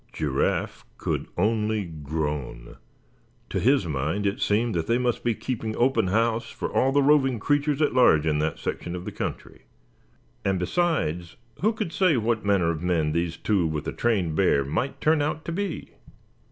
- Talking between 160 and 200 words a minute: Yes, average, 180 wpm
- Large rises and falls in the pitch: Yes, wide, 8.2 semitones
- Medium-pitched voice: No, low, 105 Hz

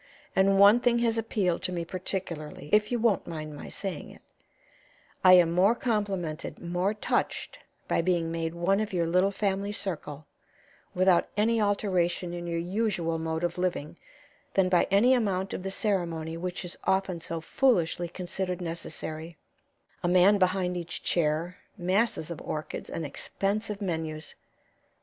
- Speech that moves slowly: No, average, 155 wpm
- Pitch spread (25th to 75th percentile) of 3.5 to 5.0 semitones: No, average, 3.0 semitones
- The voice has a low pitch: No, medium, 180 Hz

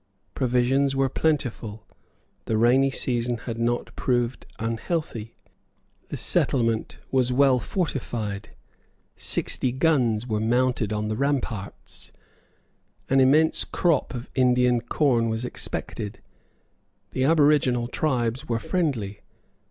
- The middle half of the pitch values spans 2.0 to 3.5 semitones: Yes, average, 2.9 semitones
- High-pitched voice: No, low, 125 Hz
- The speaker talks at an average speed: No, slow, 105 wpm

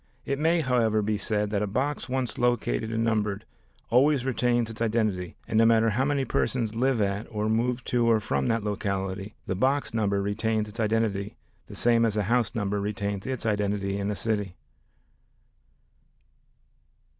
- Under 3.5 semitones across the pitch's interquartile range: Yes, average, 2.8 semitones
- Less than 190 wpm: Yes, average, 170 wpm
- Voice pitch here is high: No, low, 110 Hz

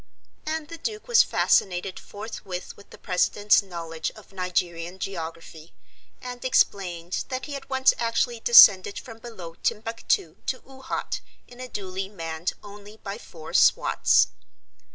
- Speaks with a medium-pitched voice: No, high, 200 Hz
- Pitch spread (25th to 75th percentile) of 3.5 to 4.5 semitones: No, average, 5.3 semitones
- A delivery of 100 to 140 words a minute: Yes, slow, 135 wpm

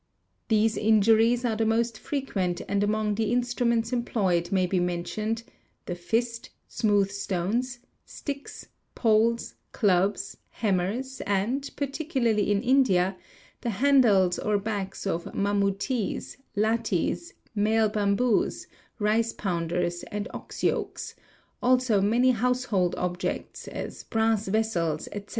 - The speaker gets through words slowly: Yes, slow, 120 wpm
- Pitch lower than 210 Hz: No, high, 215 Hz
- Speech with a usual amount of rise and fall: Yes, average, 3.2 semitones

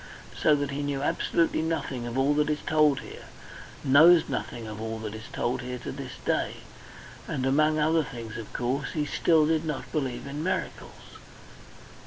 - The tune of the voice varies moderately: Yes, average, 3.8 semitones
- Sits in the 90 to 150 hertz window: Yes, medium, 140 Hz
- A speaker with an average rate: Yes, average, 180 wpm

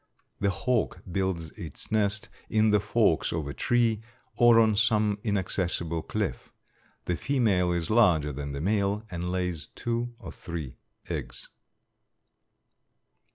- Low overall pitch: Yes, low, 100 Hz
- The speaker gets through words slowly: Yes, slow, 130 wpm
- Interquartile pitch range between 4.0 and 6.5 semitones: Yes, average, 4.4 semitones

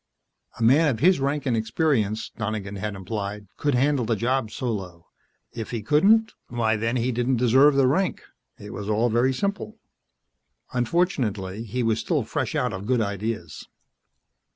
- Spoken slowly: No, average, 160 wpm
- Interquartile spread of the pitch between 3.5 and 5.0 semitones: Yes, average, 4.0 semitones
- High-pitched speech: No, low, 115 Hz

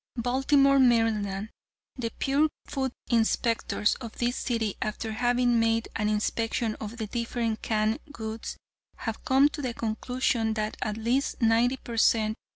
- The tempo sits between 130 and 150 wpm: Yes, average, 145 wpm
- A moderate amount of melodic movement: No, narrow, 2.2 semitones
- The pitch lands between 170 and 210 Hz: No, high, 230 Hz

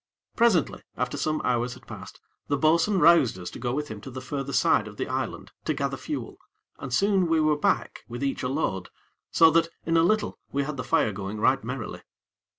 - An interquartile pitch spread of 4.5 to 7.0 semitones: Yes, average, 4.9 semitones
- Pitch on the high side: No, medium, 140 Hz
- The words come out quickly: Yes, fast, 215 wpm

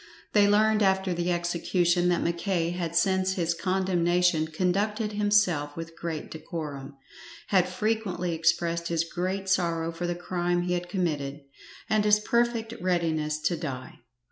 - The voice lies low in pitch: No, medium, 175 Hz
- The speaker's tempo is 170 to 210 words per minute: No, average, 145 wpm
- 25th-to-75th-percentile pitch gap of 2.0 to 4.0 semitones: Yes, narrow, 2.4 semitones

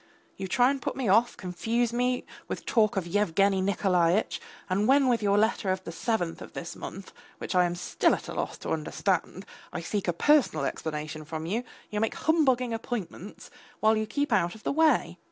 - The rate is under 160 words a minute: No, average, 200 wpm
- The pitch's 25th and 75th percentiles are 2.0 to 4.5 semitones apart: No, average, 5.2 semitones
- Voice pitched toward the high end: Yes, high, 205 Hz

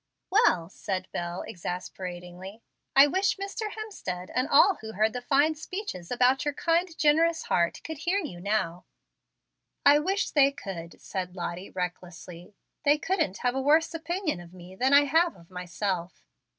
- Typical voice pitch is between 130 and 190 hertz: No, high, 245 Hz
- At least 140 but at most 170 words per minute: Yes, average, 160 wpm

